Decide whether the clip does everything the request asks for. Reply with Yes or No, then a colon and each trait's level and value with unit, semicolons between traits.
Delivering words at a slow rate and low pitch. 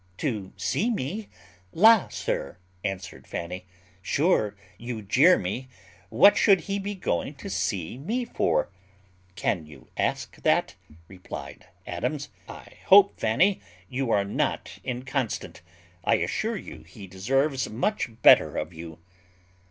Yes: slow, 130 wpm; low, 125 Hz